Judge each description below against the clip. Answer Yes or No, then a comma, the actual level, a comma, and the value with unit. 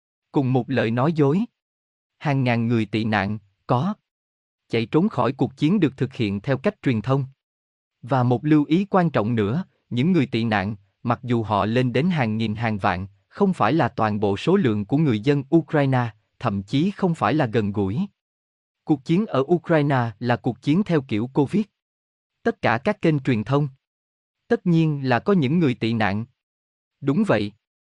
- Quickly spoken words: No, average, 185 wpm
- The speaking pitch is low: Yes, low, 125 Hz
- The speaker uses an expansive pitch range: Yes, wide, 6.1 semitones